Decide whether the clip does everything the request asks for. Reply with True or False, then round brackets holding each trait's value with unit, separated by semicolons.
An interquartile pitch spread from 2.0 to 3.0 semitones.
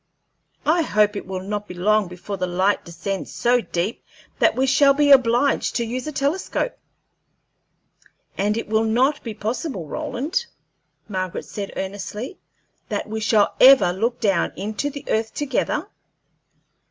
False (5.2 semitones)